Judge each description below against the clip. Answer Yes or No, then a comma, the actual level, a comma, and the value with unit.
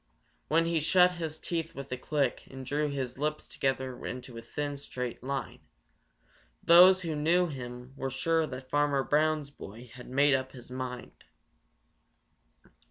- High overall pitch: No, medium, 140 Hz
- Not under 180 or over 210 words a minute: No, average, 155 wpm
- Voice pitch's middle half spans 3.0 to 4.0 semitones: Yes, average, 3.5 semitones